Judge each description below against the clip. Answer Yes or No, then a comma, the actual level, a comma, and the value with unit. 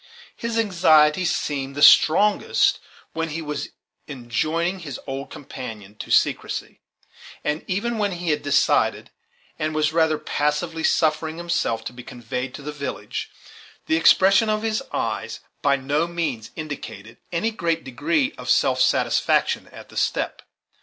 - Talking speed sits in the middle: Yes, average, 145 wpm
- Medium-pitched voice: Yes, medium, 155 Hz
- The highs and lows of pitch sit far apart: No, average, 3.8 semitones